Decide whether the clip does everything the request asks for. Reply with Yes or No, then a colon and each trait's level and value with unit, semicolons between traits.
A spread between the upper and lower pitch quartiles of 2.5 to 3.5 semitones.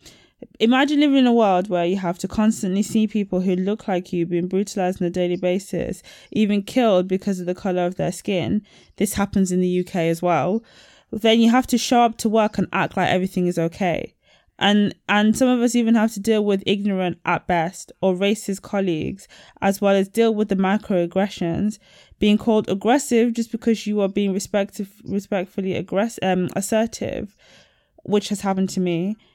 Yes: average, 2.9 semitones